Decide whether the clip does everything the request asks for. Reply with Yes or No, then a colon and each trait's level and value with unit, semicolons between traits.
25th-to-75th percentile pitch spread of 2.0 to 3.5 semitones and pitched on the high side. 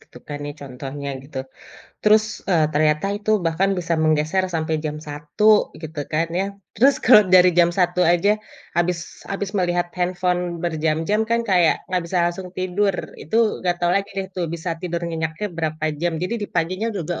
No: average, 3.1 semitones; medium, 175 Hz